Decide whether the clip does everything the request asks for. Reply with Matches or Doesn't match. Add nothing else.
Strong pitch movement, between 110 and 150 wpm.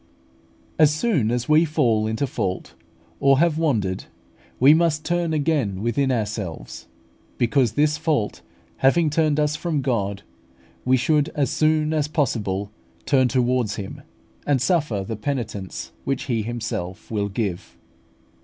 Matches